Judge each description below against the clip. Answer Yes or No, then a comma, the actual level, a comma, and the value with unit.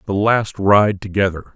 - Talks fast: No, average, 155 wpm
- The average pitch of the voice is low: Yes, low, 100 Hz